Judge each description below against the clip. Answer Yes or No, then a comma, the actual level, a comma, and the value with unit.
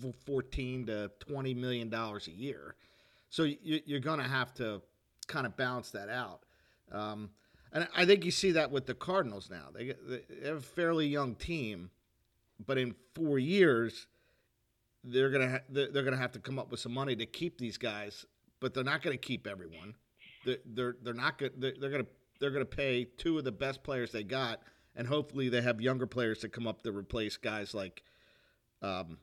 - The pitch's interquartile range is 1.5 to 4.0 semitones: Yes, average, 3.5 semitones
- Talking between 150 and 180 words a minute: No, average, 190 wpm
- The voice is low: Yes, low, 125 Hz